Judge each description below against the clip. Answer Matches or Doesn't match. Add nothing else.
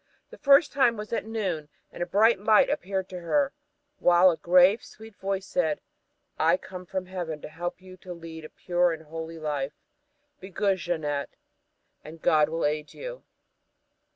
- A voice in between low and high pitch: Matches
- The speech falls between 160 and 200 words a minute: Matches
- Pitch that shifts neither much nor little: Matches